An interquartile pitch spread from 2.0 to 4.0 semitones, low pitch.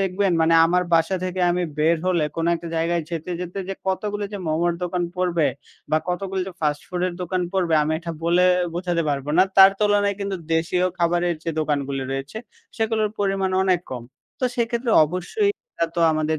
No: average, 2.7 semitones; medium, 175 Hz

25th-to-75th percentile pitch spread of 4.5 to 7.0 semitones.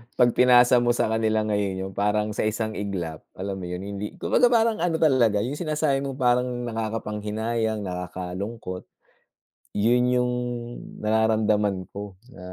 No: average, 3.4 semitones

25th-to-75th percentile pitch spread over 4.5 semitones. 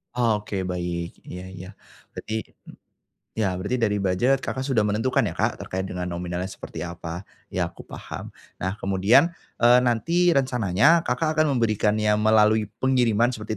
Yes: average, 4.9 semitones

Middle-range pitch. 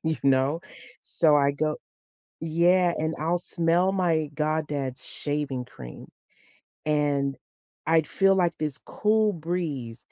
Yes: medium, 155 Hz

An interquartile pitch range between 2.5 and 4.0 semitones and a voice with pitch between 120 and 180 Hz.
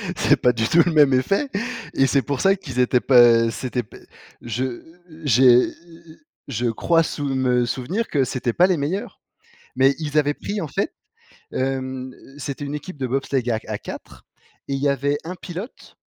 Yes: average, 3.4 semitones; low, 135 Hz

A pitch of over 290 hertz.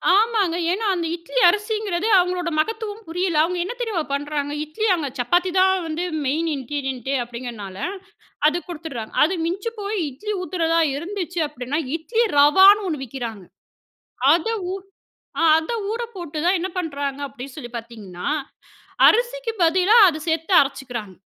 Yes: very high, 330 Hz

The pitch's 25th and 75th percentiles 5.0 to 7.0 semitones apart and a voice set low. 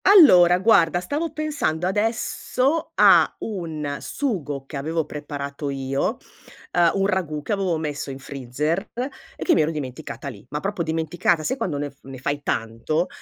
No: average, 5.3 semitones; medium, 160 Hz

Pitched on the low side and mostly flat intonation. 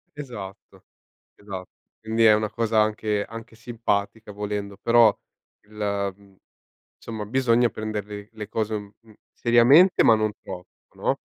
Yes: low, 110 Hz; narrow, 2.0 semitones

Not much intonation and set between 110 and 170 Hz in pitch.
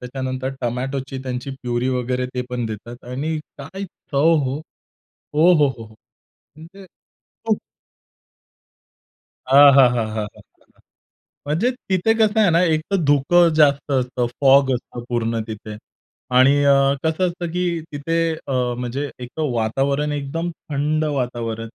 No: average, 4.2 semitones; medium, 140 Hz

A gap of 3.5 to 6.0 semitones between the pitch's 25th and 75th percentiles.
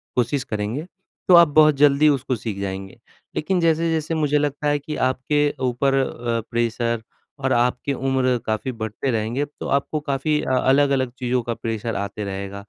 Yes: average, 4.2 semitones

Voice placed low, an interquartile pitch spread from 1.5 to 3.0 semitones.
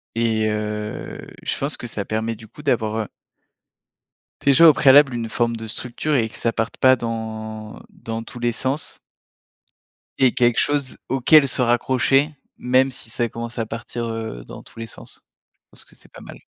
Yes: low, 115 Hz; average, 2.7 semitones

